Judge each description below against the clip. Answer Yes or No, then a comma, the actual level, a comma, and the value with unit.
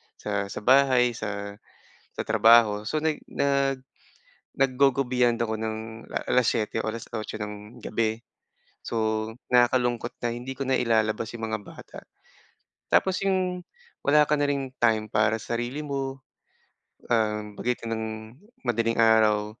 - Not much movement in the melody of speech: No, average, 3.2 semitones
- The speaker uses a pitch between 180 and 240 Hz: No, low, 115 Hz